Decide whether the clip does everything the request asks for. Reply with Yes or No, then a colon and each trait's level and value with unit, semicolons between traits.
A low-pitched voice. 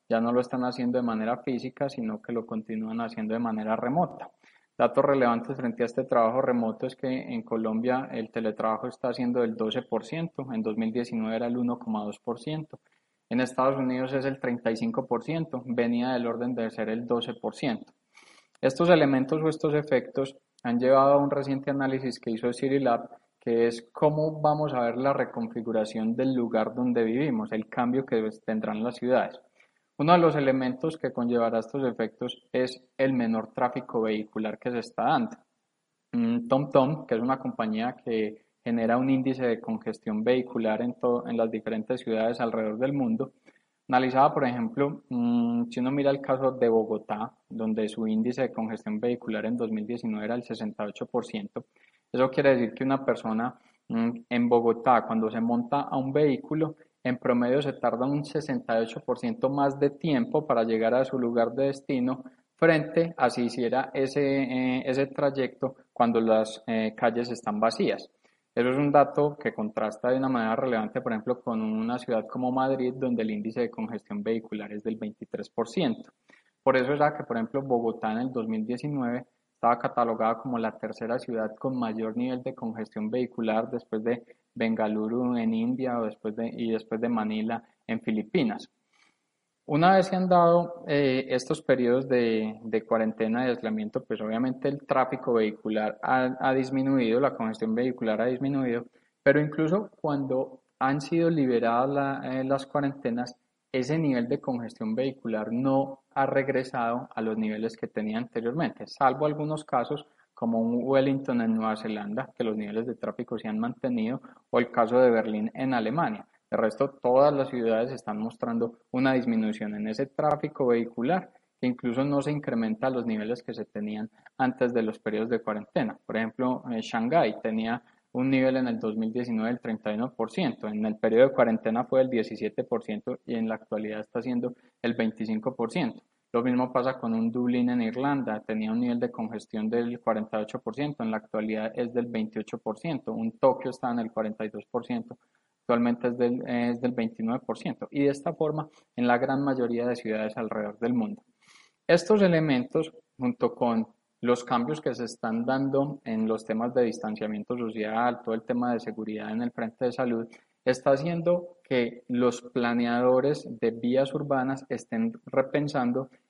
Yes: low, 125 Hz